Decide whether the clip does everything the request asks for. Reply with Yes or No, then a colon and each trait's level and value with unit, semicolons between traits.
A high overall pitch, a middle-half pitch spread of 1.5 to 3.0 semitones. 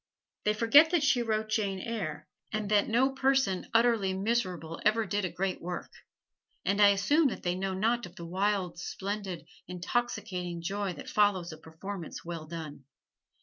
No: high, 200 Hz; average, 3.9 semitones